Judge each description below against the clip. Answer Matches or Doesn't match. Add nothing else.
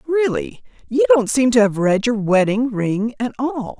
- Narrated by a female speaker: Matches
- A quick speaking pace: Doesn't match